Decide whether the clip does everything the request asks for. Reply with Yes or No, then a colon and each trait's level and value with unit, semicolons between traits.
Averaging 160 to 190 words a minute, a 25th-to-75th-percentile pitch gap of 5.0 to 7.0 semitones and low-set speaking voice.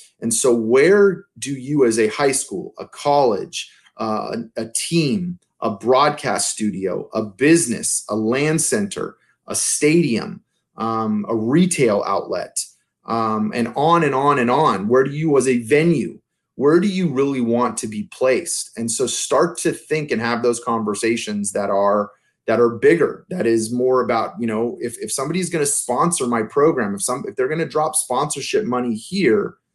Yes: average, 175 wpm; average, 5.3 semitones; low, 125 Hz